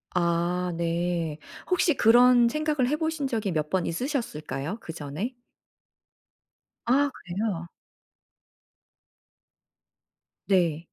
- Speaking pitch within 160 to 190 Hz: Yes, medium, 185 Hz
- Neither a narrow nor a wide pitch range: No, wide, 6.9 semitones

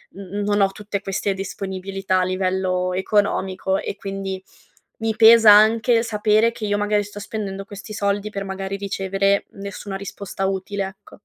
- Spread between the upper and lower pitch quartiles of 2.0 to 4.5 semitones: No, narrow, 1.3 semitones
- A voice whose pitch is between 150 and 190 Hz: No, high, 200 Hz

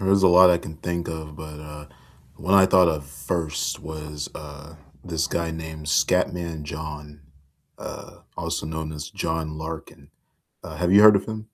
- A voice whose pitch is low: Yes, very low, 80 Hz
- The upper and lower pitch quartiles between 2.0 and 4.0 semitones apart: Yes, narrow, 2.6 semitones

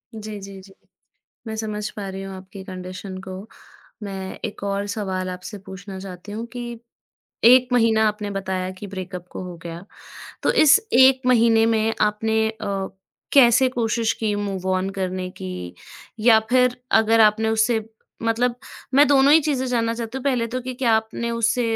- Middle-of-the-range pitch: No, high, 215 Hz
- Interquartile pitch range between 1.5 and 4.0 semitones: Yes, average, 3.4 semitones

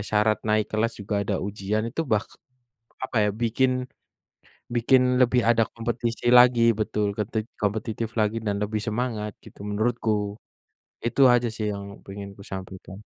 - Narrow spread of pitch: Yes, narrow, 2.2 semitones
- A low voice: Yes, low, 110 Hz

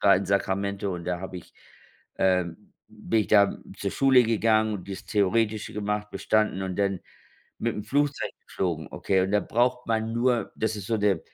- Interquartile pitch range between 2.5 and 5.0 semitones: Yes, average, 2.8 semitones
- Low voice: Yes, low, 105 Hz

